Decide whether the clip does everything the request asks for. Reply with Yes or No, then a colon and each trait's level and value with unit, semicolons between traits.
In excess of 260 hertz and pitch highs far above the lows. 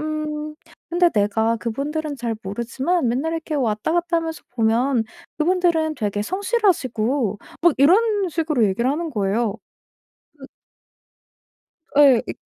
Yes: very high, 285 Hz; wide, 6.2 semitones